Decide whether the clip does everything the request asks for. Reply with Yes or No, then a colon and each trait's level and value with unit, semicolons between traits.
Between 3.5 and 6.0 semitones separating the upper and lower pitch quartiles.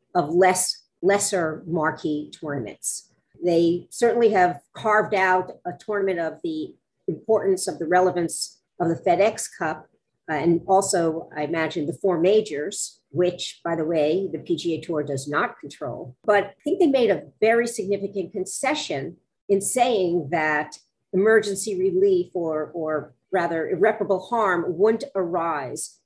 Yes: average, 3.9 semitones